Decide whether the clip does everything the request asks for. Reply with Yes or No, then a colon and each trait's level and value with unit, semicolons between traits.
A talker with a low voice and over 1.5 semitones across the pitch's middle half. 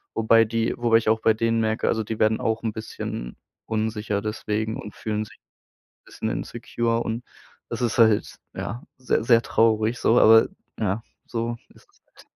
No: low, 110 Hz; narrow, 1.0 semitones